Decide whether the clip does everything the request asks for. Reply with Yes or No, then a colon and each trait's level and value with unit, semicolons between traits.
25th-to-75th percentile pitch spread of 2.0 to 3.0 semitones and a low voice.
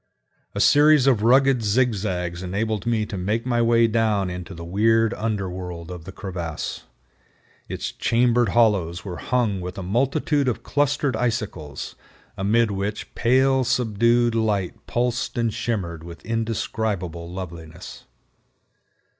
No: average, 4.6 semitones; low, 110 Hz